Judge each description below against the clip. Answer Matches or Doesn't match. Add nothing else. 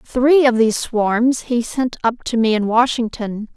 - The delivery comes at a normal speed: Matches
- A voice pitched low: Doesn't match